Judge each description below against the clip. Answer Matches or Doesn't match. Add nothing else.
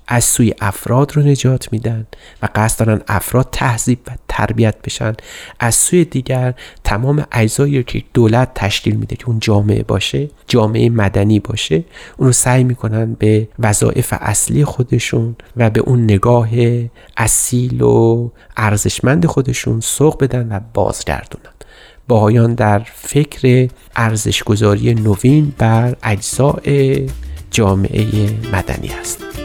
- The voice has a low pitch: Matches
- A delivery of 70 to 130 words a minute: Matches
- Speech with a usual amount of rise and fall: Matches